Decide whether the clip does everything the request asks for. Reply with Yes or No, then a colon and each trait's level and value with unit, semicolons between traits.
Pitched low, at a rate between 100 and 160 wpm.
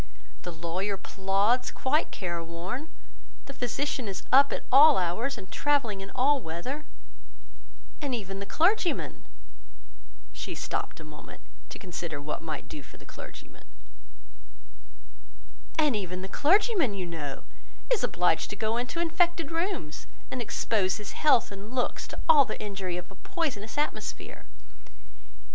No: high, 205 Hz; average, 140 wpm